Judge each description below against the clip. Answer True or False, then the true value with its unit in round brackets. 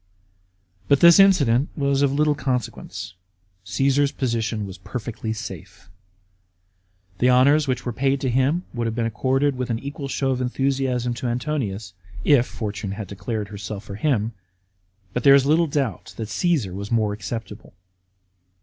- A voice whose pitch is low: True (125 Hz)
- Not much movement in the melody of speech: False (4.2 semitones)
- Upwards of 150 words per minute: True (160 wpm)